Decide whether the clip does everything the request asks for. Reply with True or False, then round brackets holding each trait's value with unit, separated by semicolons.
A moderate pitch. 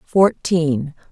True (160 Hz)